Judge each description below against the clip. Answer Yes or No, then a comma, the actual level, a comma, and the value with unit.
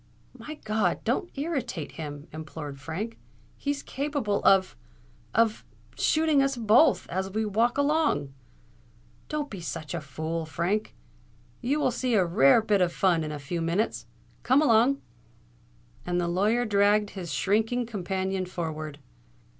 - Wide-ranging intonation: Yes, wide, 6.8 semitones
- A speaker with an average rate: No, slow, 130 wpm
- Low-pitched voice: No, high, 195 Hz